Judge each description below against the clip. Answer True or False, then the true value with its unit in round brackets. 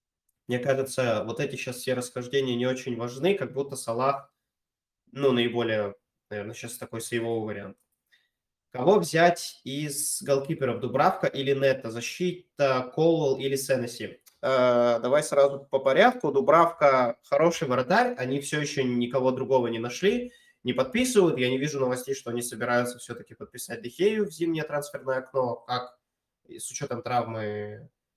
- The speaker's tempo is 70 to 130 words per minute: False (140 wpm)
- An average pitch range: True (3.4 semitones)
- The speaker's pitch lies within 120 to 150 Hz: True (130 Hz)